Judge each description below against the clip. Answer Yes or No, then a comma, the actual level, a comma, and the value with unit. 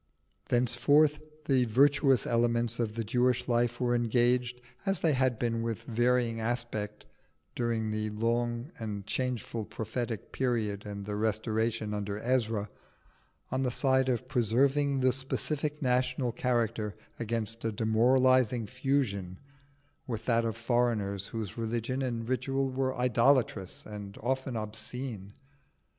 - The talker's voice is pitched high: No, low, 120 Hz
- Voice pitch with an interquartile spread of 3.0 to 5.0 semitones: No, narrow, 2.6 semitones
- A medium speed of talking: No, slow, 125 wpm